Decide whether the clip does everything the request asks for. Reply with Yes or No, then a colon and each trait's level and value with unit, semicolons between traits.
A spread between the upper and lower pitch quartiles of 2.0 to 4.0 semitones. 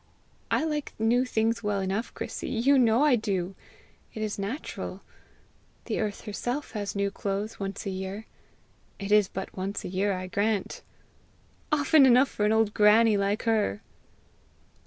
Yes: average, 2.7 semitones